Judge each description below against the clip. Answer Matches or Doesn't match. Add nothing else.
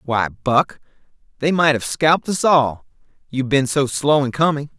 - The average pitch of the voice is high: Doesn't match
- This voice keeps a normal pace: Matches